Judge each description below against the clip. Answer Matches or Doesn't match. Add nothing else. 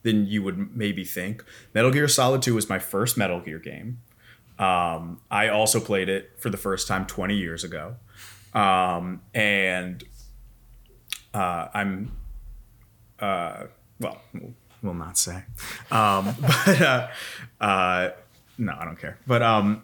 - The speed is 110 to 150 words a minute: Matches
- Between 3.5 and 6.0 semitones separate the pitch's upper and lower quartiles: Matches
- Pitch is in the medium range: Doesn't match